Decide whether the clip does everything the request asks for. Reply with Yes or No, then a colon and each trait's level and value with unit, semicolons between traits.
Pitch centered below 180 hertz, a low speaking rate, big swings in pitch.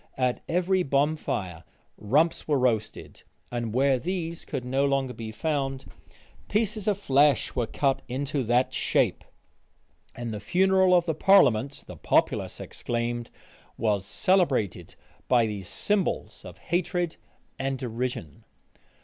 Yes: low, 135 Hz; slow, 125 wpm; wide, 6.2 semitones